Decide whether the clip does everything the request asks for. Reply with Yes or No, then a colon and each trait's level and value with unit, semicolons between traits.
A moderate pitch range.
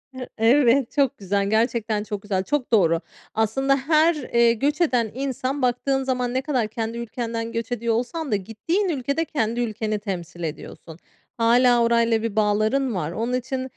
Yes: average, 3.4 semitones